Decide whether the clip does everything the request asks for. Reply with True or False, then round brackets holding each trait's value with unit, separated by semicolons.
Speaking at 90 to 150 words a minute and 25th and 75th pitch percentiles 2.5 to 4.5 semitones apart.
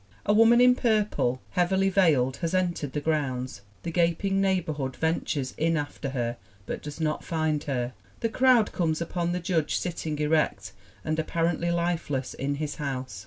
False (170 wpm; 3.8 semitones)